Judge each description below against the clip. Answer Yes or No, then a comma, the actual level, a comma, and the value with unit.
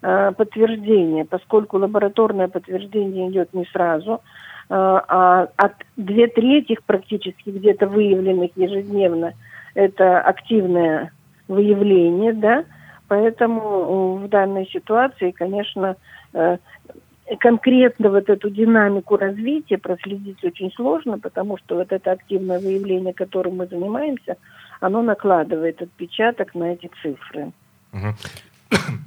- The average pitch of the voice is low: No, high, 195 Hz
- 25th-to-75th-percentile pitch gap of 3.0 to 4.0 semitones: No, narrow, 2.6 semitones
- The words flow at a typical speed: No, slow, 95 wpm